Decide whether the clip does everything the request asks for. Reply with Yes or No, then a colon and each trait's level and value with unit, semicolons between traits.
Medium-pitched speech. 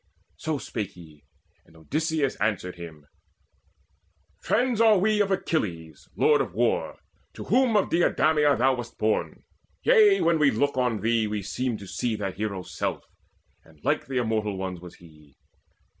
No: low, 115 Hz